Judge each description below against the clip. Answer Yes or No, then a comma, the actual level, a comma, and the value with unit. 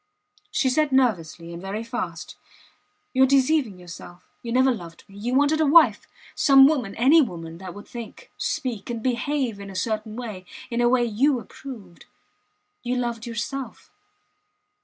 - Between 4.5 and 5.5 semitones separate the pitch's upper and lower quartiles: Yes, average, 5.0 semitones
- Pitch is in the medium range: No, high, 235 Hz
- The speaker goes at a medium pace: Yes, average, 160 wpm